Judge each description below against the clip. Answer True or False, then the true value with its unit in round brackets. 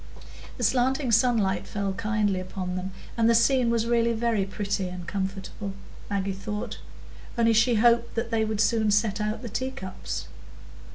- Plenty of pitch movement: False (3.1 semitones)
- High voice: True (215 Hz)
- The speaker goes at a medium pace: True (160 wpm)